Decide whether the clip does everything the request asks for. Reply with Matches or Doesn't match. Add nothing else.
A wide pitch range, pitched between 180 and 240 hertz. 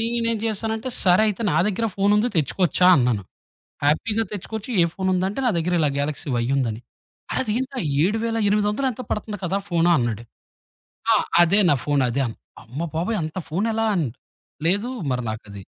Matches